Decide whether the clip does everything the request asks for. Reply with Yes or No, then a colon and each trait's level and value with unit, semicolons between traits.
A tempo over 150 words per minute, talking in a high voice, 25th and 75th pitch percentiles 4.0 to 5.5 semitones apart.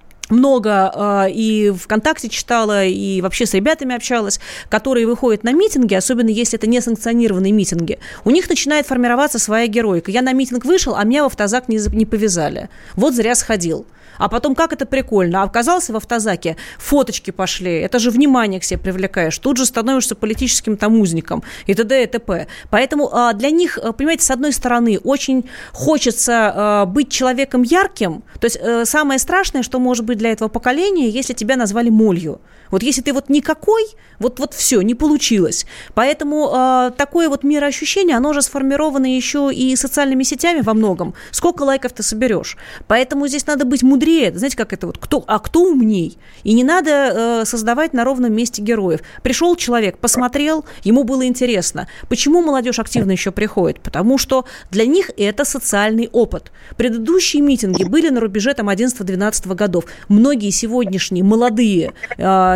Yes: fast, 160 wpm; high, 240 Hz; average, 4.5 semitones